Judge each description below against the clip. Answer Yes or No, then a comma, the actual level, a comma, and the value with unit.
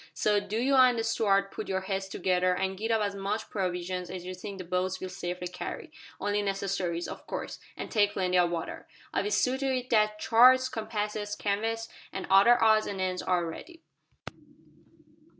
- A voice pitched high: Yes, high, 200 Hz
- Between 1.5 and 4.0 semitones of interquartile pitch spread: Yes, average, 3.2 semitones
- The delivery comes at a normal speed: Yes, average, 185 wpm